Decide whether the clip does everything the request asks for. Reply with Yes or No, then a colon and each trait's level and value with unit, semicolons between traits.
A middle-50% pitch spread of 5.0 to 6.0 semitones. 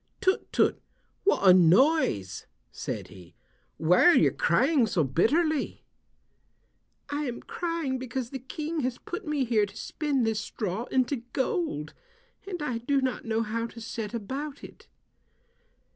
Yes: wide, 5.6 semitones